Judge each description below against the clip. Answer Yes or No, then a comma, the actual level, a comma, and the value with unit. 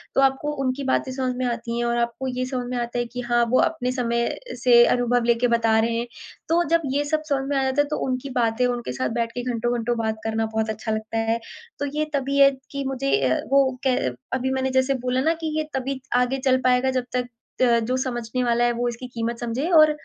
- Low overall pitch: No, very high, 250 Hz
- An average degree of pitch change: No, narrow, 2.1 semitones